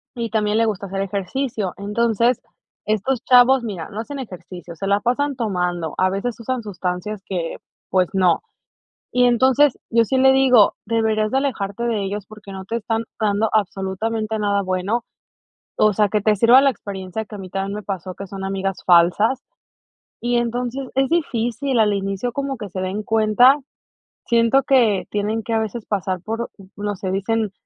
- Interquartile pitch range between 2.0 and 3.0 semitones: No, average, 3.5 semitones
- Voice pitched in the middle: No, high, 215 Hz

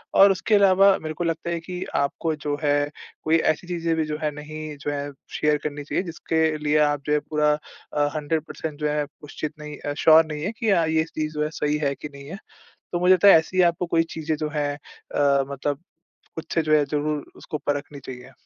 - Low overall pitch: No, medium, 150 Hz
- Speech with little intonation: Yes, narrow, 1.8 semitones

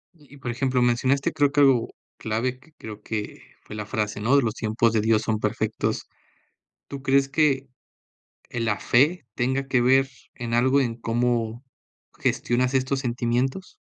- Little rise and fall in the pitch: No, average, 3.0 semitones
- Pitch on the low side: Yes, low, 125 Hz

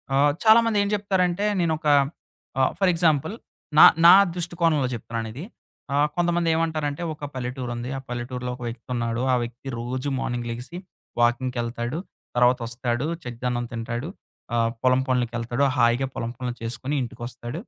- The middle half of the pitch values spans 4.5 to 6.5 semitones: Yes, average, 4.9 semitones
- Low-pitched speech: Yes, low, 125 Hz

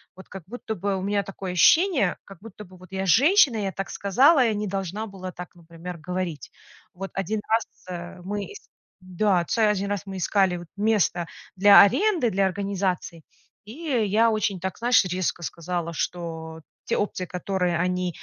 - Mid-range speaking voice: No, high, 195 Hz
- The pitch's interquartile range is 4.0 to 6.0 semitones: No, average, 2.9 semitones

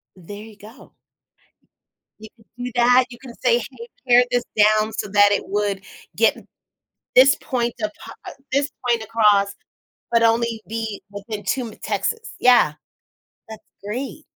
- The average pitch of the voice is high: Yes, high, 225 Hz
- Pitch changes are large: No, average, 2.8 semitones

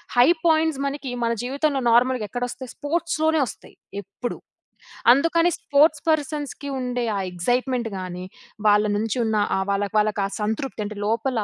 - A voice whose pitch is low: No, very high, 250 Hz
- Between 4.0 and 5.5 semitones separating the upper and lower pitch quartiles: Yes, average, 5.2 semitones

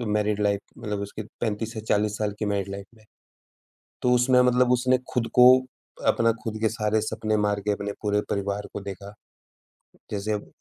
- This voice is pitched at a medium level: No, low, 105 Hz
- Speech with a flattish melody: Yes, narrow, 2.0 semitones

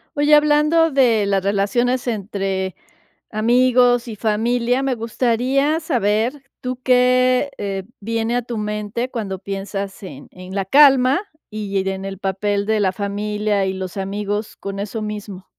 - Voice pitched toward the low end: No, high, 215 Hz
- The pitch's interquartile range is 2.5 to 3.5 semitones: No, average, 4.0 semitones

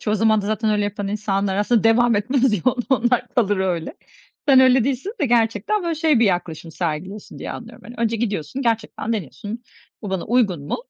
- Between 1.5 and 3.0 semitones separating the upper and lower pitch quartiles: No, average, 3.6 semitones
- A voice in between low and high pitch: No, high, 220 Hz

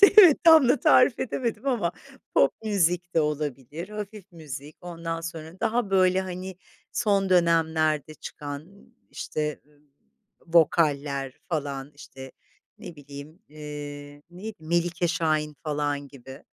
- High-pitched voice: No, medium, 165 Hz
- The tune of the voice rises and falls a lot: No, average, 4.2 semitones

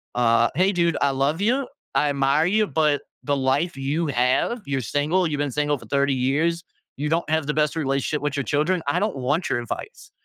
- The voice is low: No, medium, 150 Hz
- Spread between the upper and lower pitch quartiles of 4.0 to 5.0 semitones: No, average, 3.5 semitones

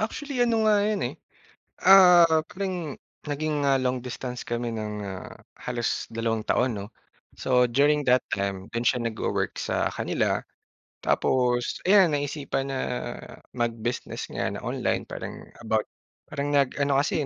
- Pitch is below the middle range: Yes, low, 130 Hz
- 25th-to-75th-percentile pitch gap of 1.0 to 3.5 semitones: No, average, 4.6 semitones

